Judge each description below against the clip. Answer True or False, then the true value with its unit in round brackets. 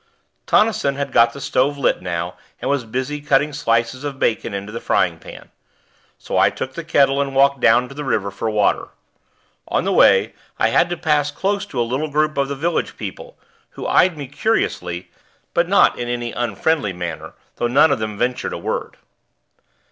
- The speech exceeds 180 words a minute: True (195 wpm)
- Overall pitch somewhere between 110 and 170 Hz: True (135 Hz)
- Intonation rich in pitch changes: False (4.2 semitones)